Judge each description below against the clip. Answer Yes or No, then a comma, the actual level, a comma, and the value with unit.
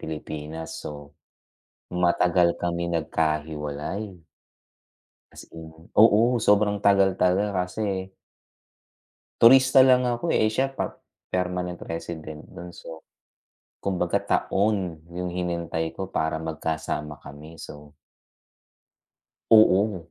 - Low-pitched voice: Yes, very low, 90 Hz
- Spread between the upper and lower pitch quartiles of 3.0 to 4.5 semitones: Yes, average, 4.0 semitones